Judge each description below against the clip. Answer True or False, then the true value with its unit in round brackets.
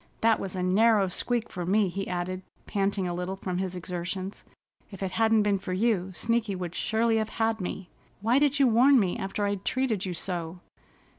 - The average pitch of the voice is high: True (195 Hz)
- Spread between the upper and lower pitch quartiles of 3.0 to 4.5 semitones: True (3.4 semitones)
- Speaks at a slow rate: False (200 wpm)